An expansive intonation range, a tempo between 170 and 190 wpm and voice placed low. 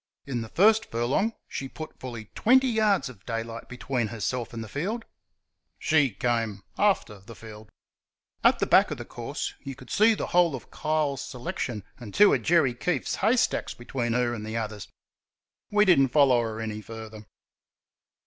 Yes: wide, 6.4 semitones; average, 175 wpm; low, 125 Hz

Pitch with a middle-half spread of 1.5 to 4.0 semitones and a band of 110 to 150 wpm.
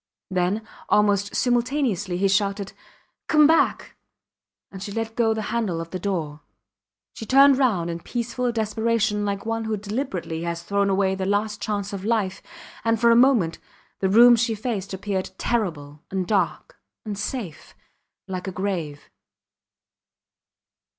Yes: average, 3.3 semitones; average, 145 wpm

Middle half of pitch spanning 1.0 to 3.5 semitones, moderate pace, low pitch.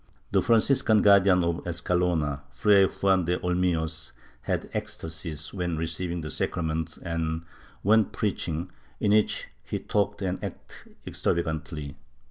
No: average, 3.2 semitones; slow, 120 wpm; very low, 85 Hz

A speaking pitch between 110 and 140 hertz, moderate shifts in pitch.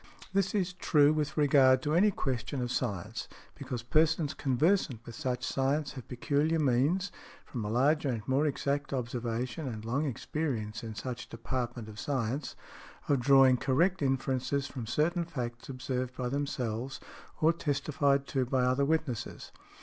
Yes: low, 135 Hz; average, 3.4 semitones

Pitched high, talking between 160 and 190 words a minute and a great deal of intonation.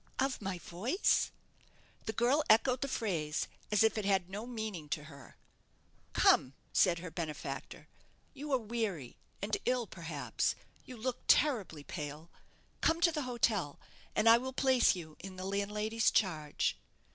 No: high, 210 Hz; average, 150 wpm; wide, 6.4 semitones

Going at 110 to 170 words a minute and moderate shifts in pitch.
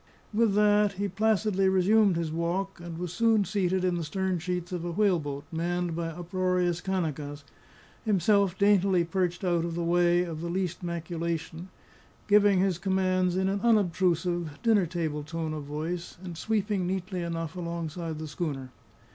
No: average, 160 wpm; narrow, 2.3 semitones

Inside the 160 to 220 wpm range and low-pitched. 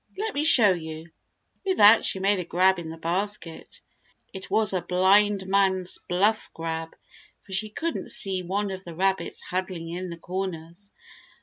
No: average, 170 wpm; high, 190 Hz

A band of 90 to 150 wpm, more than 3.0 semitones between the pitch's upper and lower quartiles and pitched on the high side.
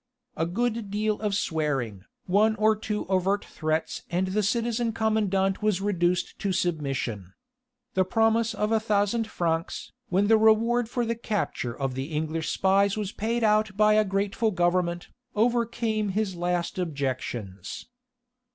Yes: average, 145 wpm; average, 4.0 semitones; high, 200 Hz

